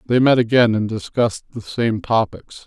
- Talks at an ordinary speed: Yes, average, 180 wpm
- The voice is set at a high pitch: No, low, 115 Hz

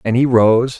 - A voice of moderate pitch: No, low, 120 Hz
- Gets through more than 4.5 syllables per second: No, 4.4 syllables/s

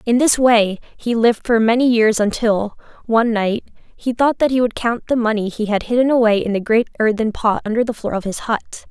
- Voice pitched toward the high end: Yes, high, 225 Hz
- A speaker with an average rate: No, fast, 230 wpm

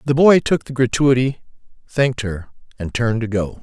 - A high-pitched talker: No, low, 120 Hz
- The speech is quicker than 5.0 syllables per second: Yes, 5.5 syllables/s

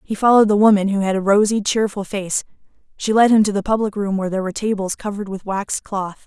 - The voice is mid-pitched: No, high, 205 Hz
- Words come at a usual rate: No, fast, 240 wpm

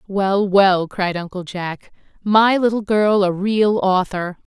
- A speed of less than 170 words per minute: Yes, average, 145 wpm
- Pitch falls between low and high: No, high, 195 Hz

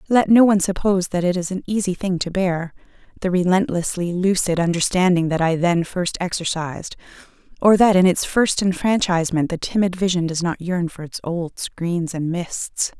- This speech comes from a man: No, female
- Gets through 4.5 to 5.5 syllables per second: Yes, 5.1 syllables/s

